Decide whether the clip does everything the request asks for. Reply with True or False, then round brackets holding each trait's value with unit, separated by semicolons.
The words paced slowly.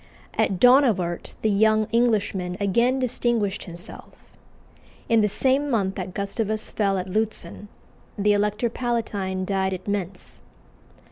True (125 wpm)